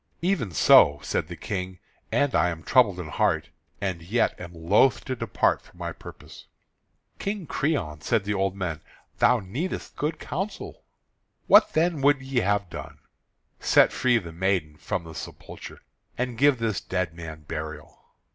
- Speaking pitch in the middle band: No, low, 100 Hz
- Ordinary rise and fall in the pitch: No, wide, 7.6 semitones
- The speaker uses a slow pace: No, average, 160 wpm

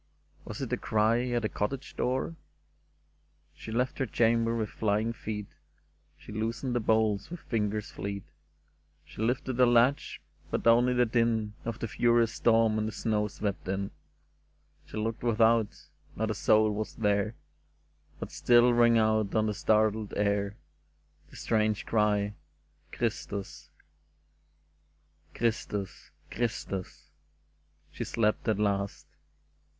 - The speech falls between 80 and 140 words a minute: Yes, slow, 135 wpm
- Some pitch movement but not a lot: No, narrow, 2.3 semitones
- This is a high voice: No, low, 110 Hz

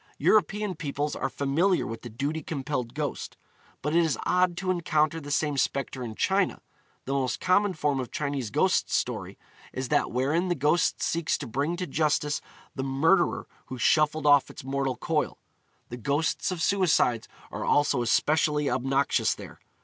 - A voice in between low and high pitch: Yes, medium, 145 Hz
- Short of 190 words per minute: Yes, average, 165 wpm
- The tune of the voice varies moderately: Yes, average, 3.7 semitones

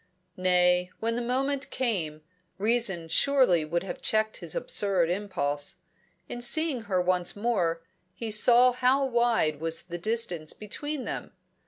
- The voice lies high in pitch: Yes, high, 210 Hz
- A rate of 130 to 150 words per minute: Yes, average, 140 wpm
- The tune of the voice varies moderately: No, wide, 5.7 semitones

